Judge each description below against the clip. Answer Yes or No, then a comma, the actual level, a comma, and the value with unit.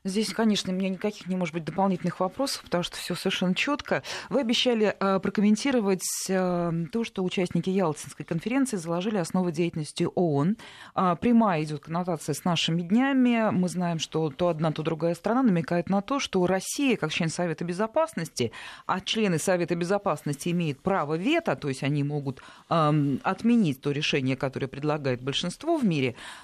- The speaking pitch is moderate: Yes, medium, 180 Hz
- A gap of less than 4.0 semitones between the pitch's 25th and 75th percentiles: No, average, 4.3 semitones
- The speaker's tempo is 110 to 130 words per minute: No, average, 155 wpm